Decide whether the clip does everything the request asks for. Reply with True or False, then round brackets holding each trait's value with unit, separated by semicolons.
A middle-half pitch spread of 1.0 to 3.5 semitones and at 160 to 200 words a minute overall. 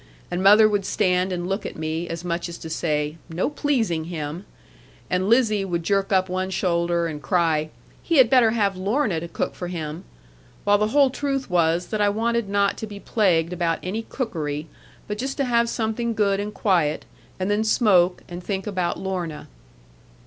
False (4.0 semitones; 190 wpm)